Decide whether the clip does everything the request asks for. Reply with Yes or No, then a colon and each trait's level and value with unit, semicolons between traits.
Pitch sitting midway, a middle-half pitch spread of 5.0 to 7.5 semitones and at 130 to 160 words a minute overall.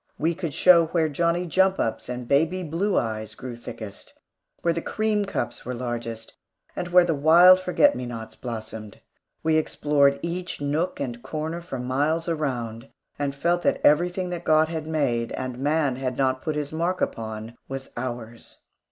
No: medium, 150 Hz; wide, 5.6 semitones; average, 170 wpm